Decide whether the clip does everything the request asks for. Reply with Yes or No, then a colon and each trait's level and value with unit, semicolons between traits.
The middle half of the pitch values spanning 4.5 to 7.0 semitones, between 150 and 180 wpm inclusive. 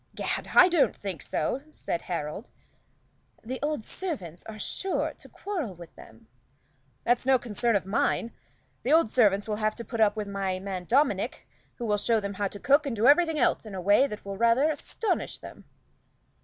No: wide, 5.4 semitones; average, 190 wpm